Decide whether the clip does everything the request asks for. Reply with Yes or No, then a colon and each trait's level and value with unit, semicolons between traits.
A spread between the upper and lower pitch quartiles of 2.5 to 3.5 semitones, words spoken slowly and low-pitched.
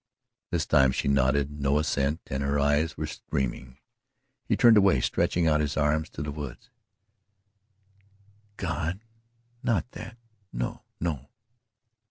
Yes: average, 3.0 semitones; slow, 130 wpm; very low, 75 Hz